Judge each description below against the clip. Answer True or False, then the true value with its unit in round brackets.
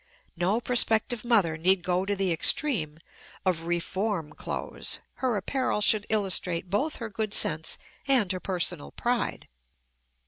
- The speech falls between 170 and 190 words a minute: False (135 wpm)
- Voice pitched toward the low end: False (195 Hz)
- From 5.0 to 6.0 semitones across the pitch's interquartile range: False (4.3 semitones)